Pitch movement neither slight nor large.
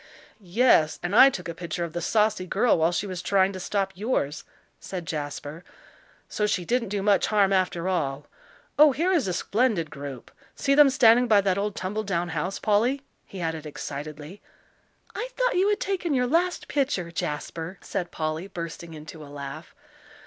No: wide, 5.8 semitones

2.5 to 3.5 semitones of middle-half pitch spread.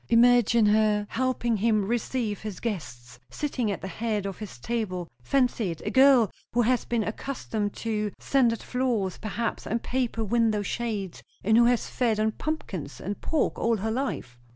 Yes: average, 2.8 semitones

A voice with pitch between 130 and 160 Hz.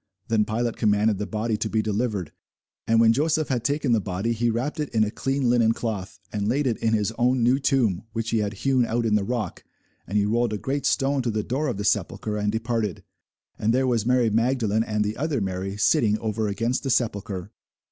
No: low, 115 Hz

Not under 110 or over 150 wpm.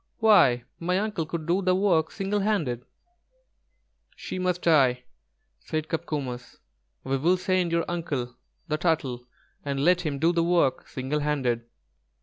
Yes: average, 140 wpm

